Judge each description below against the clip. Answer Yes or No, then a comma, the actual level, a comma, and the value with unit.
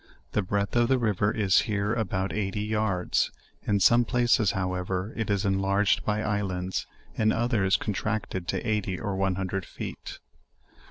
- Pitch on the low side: Yes, low, 100 Hz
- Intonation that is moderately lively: No, narrow, 2.3 semitones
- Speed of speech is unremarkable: Yes, average, 155 wpm